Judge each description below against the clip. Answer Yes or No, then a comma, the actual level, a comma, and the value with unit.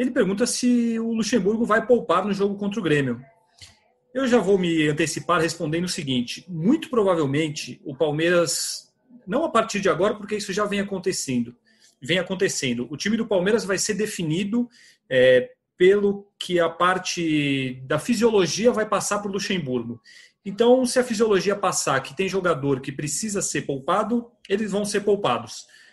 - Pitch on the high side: Yes, high, 195 Hz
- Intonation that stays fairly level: No, wide, 5.5 semitones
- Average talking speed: Yes, average, 165 wpm